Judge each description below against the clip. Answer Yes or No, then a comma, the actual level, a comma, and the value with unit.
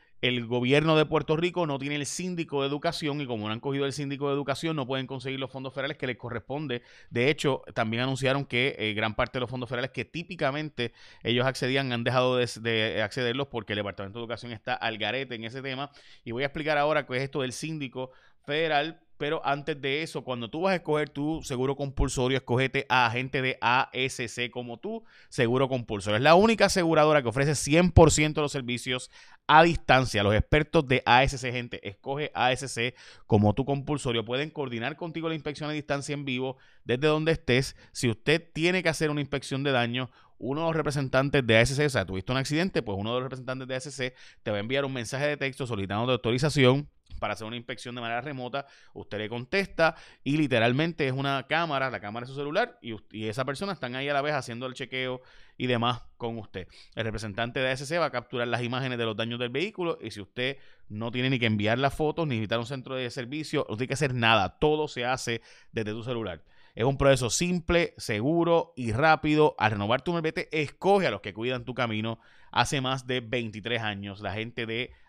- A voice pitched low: Yes, low, 130 Hz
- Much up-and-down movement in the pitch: No, average, 3.7 semitones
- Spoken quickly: Yes, fast, 215 wpm